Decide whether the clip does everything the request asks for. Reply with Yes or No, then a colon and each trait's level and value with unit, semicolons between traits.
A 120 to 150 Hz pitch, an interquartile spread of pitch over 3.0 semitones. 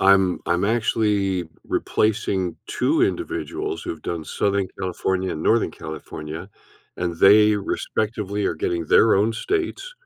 No: low, 100 Hz; average, 3.7 semitones